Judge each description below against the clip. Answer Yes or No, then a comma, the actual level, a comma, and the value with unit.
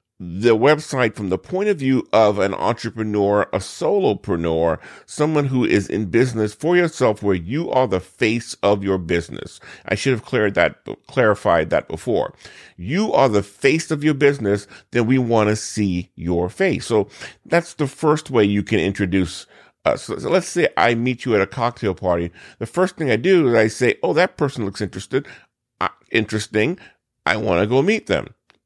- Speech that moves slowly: No, average, 185 wpm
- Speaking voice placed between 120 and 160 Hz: No, low, 110 Hz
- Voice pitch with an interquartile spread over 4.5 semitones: Yes, wide, 5.4 semitones